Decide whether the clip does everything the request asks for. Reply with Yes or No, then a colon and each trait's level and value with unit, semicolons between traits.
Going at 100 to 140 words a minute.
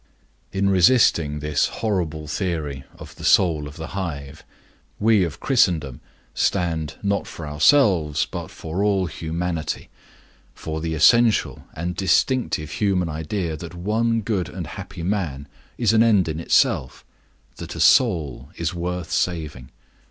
Yes: slow, 135 wpm